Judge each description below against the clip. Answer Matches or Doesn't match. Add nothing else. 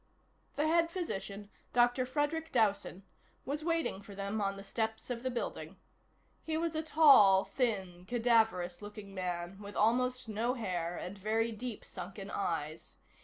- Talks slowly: Doesn't match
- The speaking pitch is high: Matches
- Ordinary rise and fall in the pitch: Matches